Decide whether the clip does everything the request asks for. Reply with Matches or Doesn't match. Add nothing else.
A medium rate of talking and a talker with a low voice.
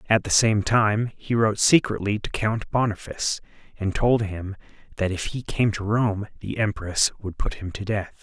Matches